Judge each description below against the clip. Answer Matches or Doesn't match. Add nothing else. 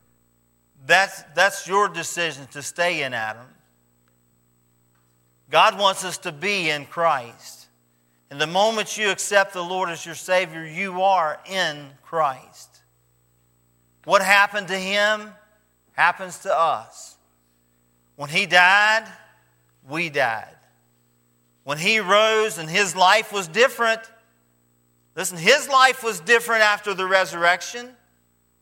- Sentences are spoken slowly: Matches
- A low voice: Doesn't match